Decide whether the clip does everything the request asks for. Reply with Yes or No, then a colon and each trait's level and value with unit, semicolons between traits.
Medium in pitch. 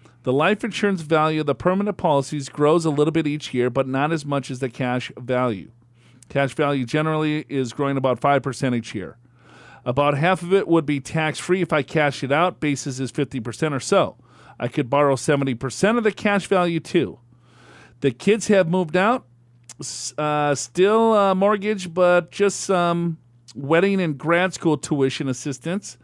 Yes: medium, 150 Hz